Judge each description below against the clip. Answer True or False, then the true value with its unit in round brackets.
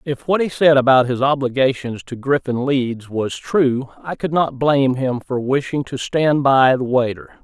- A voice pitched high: False (135 Hz)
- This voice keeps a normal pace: True (195 wpm)